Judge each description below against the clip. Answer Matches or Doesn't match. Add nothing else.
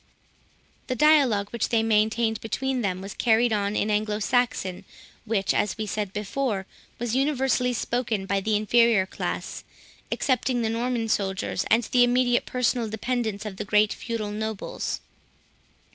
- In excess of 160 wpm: Doesn't match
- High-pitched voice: Matches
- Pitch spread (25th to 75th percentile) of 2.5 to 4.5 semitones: Matches